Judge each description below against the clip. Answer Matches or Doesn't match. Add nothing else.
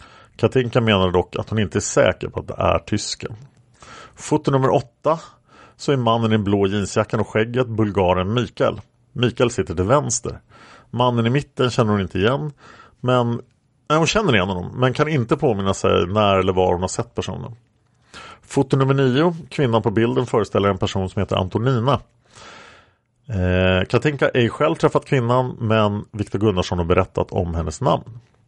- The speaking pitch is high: Doesn't match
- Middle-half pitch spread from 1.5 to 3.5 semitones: Doesn't match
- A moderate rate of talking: Matches